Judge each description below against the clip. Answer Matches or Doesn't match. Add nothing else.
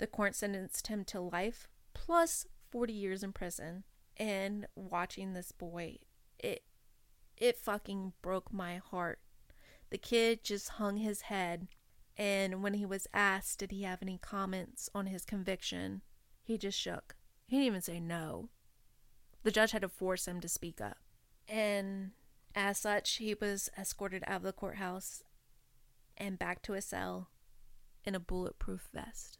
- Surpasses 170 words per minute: Doesn't match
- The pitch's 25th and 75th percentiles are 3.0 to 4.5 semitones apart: Doesn't match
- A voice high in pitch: Matches